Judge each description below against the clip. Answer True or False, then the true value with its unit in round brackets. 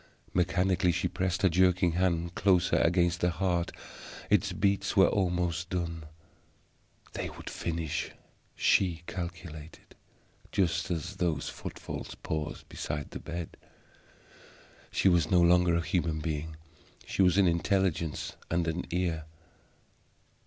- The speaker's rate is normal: False (125 wpm)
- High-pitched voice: False (85 Hz)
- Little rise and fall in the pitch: True (1.7 semitones)